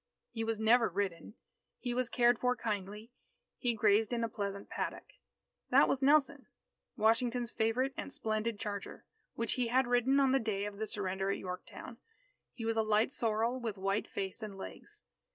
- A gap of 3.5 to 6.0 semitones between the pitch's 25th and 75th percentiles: No, average, 2.9 semitones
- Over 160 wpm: Yes, average, 175 wpm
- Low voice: No, high, 225 Hz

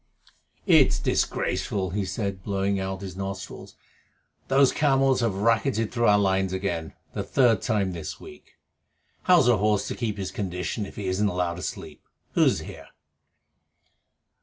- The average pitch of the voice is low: Yes, low, 100 Hz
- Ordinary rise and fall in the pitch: Yes, average, 3.3 semitones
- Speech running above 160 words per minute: No, average, 150 wpm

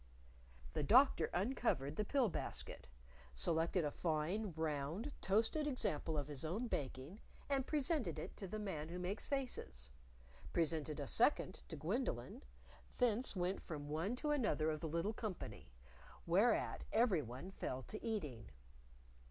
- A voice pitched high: No, medium, 180 Hz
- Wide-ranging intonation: Yes, wide, 6.8 semitones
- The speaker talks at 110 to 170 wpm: Yes, average, 140 wpm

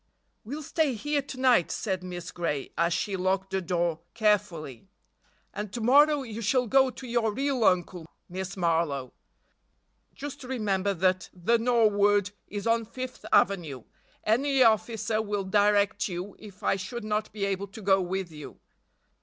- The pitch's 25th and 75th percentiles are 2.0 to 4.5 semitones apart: Yes, average, 4.2 semitones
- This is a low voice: No, high, 205 Hz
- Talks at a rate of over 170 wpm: No, average, 155 wpm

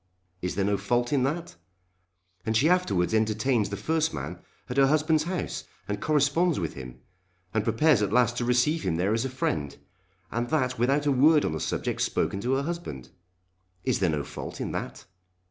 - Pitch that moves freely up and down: Yes, wide, 7.0 semitones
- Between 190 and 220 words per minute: Yes, average, 195 wpm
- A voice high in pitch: No, low, 120 Hz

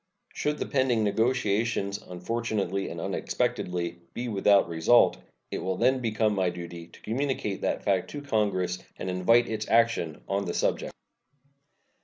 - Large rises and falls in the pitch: No, average, 4.2 semitones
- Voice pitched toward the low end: Yes, low, 105 Hz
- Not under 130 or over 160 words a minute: Yes, average, 145 wpm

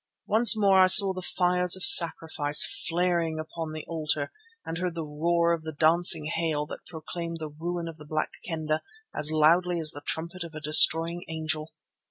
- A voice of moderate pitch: Yes, medium, 165 Hz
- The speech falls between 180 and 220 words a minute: Yes, average, 185 wpm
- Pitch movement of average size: No, narrow, 2.1 semitones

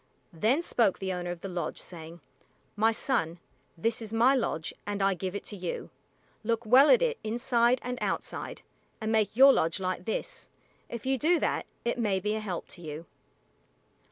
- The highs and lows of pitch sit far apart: No, average, 4.7 semitones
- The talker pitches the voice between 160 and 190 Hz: No, high, 215 Hz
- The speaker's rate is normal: Yes, average, 185 wpm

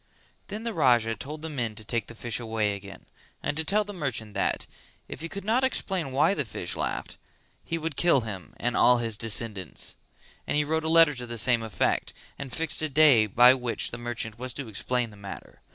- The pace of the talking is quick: Yes, fast, 215 wpm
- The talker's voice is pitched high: No, low, 125 Hz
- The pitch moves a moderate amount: No, wide, 5.7 semitones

